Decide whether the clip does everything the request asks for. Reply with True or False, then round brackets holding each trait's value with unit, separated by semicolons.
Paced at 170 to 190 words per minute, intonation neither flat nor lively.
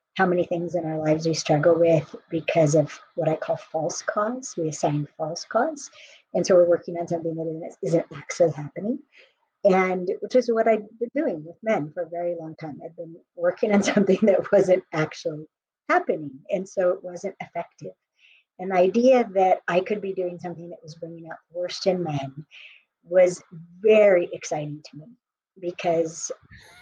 True (175 wpm; 3.4 semitones)